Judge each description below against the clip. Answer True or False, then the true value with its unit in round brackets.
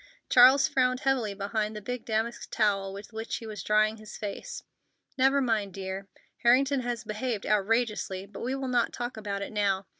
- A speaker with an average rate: True (180 wpm)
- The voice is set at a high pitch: True (220 Hz)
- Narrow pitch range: False (3.5 semitones)